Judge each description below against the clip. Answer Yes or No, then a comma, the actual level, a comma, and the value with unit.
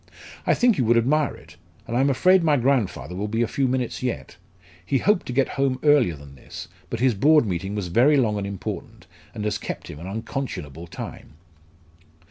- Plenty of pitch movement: Yes, wide, 5.7 semitones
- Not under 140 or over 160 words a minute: No, fast, 205 wpm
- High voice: No, low, 120 Hz